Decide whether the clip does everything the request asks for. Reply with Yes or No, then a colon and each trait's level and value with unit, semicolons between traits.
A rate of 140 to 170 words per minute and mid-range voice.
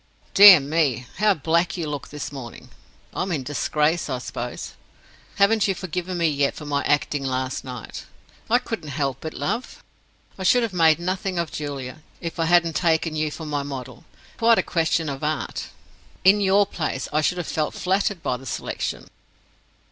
No: average, 180 wpm; medium, 160 Hz